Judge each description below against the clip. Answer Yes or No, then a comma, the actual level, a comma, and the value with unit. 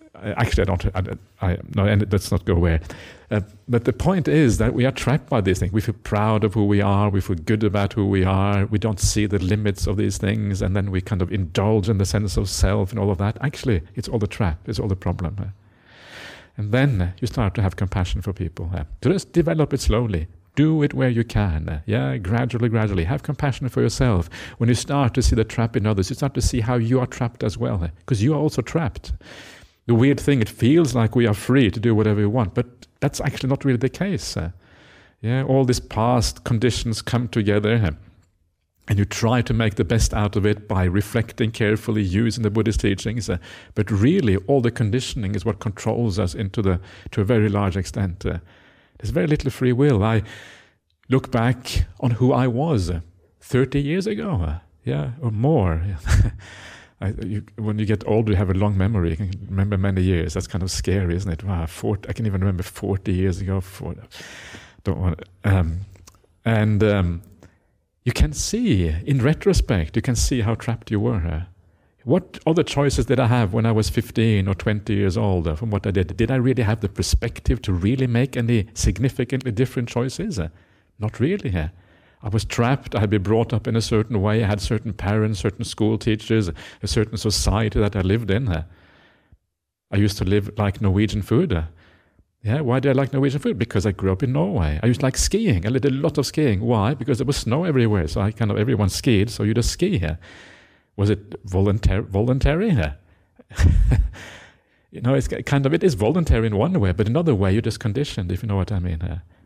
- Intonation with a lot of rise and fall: No, average, 4.1 semitones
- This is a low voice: Yes, low, 105 Hz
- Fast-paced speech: Yes, fast, 215 wpm